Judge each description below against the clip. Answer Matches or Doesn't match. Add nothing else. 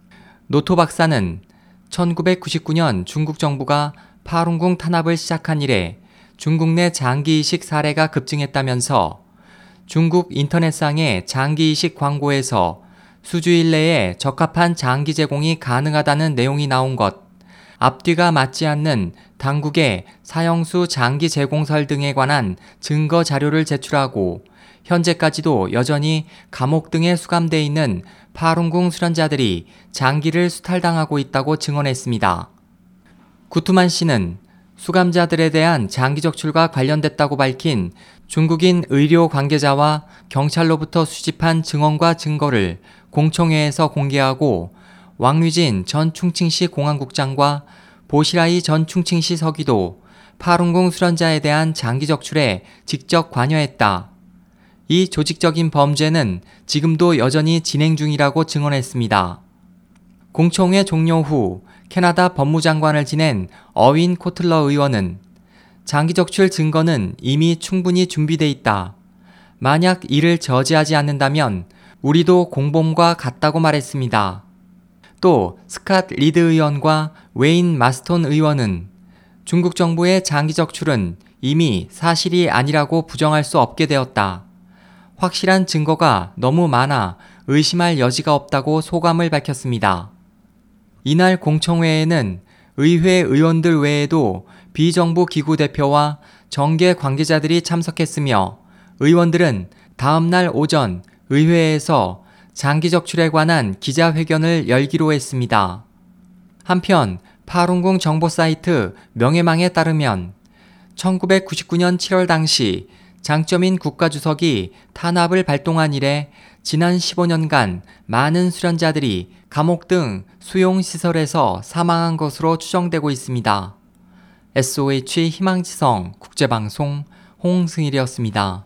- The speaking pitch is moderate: Matches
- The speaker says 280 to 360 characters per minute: Doesn't match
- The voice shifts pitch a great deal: Doesn't match